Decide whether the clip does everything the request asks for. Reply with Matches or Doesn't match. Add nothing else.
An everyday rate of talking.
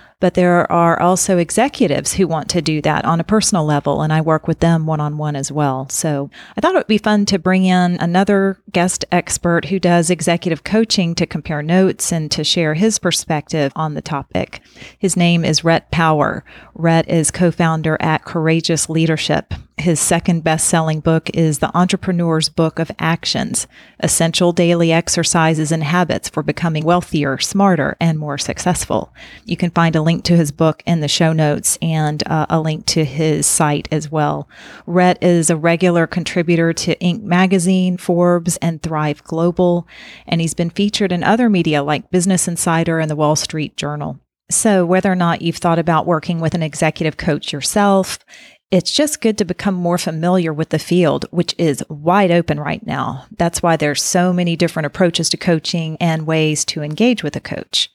Matches